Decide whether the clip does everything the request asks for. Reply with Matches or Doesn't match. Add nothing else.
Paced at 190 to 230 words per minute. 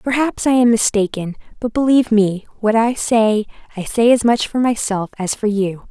Matches